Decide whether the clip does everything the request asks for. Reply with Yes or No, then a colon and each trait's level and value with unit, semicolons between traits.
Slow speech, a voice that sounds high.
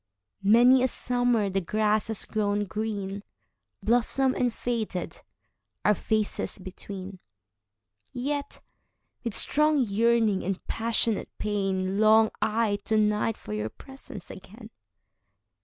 Yes: slow, 100 wpm; high, 215 Hz